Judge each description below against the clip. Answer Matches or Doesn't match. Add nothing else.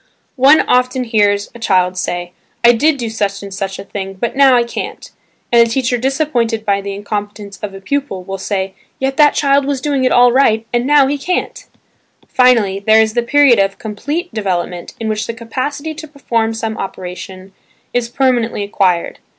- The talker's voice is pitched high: Matches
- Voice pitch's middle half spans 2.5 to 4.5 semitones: Doesn't match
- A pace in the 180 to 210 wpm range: Matches